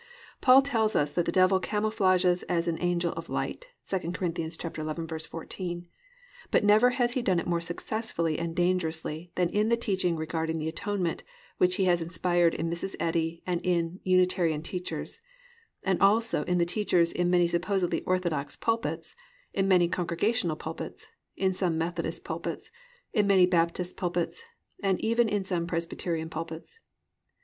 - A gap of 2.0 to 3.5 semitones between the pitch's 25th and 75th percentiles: Yes, narrow, 2.5 semitones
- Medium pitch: Yes, medium, 175 Hz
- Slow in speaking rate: No, average, 155 wpm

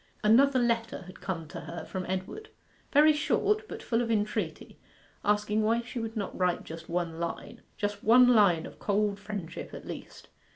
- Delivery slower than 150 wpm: No, average, 175 wpm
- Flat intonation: No, average, 4.3 semitones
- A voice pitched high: Yes, high, 210 Hz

